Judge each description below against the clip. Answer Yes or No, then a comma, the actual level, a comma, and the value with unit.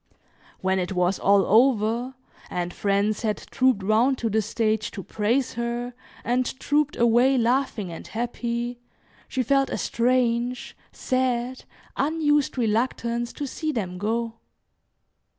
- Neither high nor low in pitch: No, high, 235 Hz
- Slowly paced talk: Yes, slow, 130 wpm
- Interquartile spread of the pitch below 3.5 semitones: Yes, average, 3.0 semitones